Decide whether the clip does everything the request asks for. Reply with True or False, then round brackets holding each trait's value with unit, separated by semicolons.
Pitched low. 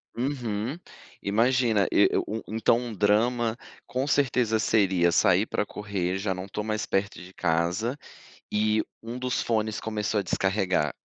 True (110 Hz)